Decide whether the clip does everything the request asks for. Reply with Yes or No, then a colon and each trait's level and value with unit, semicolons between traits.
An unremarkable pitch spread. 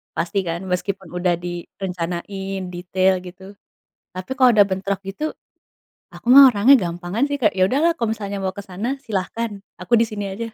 Yes: average, 3.4 semitones